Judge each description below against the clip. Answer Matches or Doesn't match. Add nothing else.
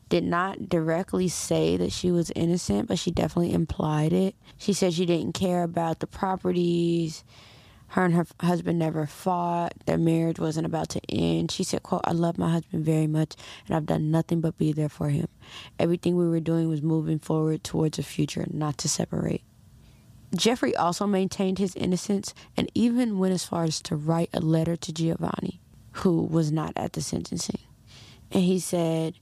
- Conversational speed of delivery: Matches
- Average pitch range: Doesn't match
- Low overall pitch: Doesn't match